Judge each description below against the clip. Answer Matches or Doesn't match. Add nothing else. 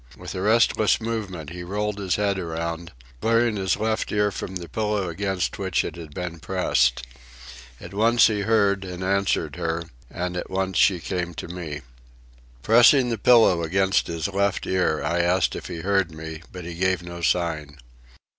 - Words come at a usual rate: Matches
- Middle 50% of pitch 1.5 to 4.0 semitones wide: Matches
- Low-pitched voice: Matches